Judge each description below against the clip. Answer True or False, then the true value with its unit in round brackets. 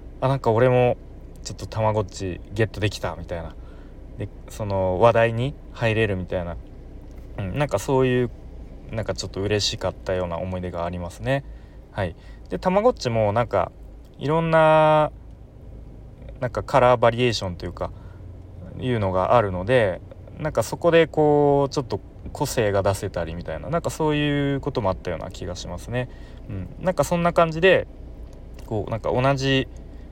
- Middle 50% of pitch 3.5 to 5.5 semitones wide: False (6.6 semitones)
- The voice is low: True (110 Hz)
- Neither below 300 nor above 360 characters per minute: True (350 characters per minute)